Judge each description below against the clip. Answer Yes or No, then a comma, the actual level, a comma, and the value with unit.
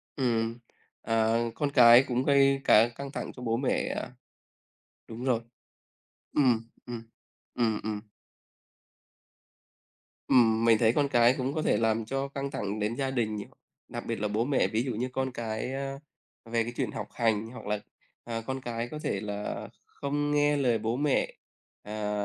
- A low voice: Yes, low, 120 Hz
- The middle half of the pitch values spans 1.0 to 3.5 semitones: Yes, average, 3.2 semitones